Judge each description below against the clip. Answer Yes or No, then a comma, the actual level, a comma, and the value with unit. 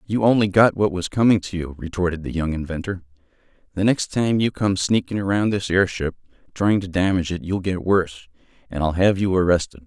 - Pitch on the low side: Yes, very low, 95 Hz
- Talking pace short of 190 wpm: No, average, 200 wpm